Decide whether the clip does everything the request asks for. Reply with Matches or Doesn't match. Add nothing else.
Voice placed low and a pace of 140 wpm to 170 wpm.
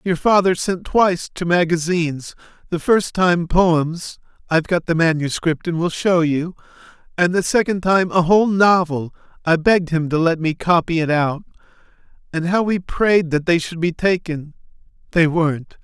Doesn't match